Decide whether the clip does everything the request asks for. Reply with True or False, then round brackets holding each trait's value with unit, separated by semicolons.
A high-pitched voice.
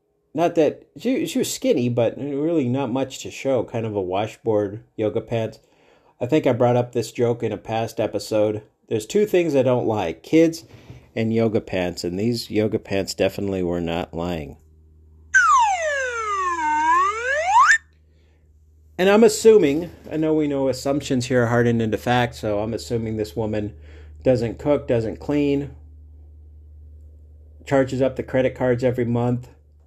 False (120 Hz)